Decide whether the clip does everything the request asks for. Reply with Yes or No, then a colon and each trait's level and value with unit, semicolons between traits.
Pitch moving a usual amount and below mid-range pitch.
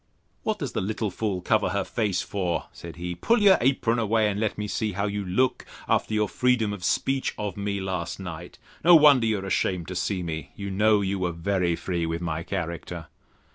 Yes: average, 3.6 semitones; low, 100 Hz